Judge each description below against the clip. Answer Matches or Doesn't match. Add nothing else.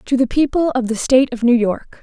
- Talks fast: Matches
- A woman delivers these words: Matches